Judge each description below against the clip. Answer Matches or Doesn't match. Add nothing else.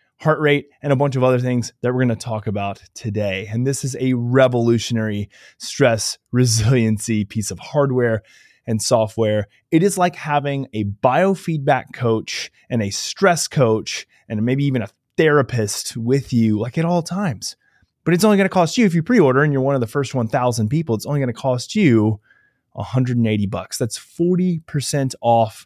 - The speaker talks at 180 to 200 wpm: Matches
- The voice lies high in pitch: Doesn't match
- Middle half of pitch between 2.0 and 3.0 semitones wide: Doesn't match